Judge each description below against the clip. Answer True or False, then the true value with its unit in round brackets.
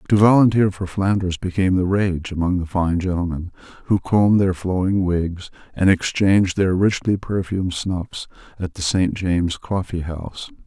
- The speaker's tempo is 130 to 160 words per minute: True (150 wpm)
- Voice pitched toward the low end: True (90 Hz)